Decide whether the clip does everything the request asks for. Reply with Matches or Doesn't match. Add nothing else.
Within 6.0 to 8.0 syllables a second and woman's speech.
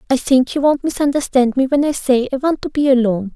Matches